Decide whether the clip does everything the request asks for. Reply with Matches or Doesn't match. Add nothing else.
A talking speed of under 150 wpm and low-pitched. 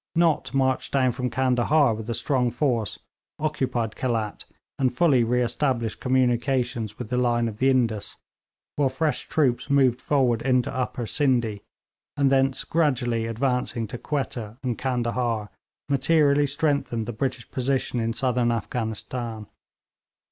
Matches